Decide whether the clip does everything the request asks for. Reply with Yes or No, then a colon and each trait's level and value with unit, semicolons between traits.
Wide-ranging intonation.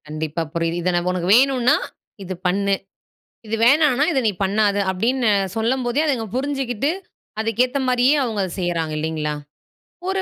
Yes: wide, 6.4 semitones